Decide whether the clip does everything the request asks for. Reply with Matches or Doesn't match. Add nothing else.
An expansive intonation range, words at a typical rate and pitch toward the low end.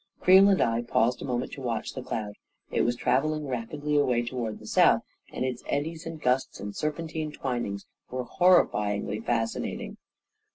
Doesn't match